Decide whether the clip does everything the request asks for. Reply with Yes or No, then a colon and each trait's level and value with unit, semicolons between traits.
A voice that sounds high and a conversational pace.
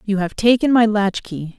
Yes: high, 210 Hz; average, 190 wpm